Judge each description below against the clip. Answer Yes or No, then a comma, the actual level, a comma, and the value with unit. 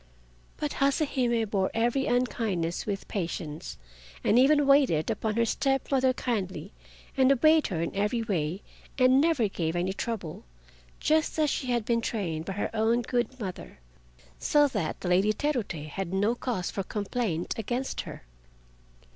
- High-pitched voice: Yes, high, 225 Hz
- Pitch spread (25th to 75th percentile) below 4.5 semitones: No, wide, 5.5 semitones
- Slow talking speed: No, average, 155 wpm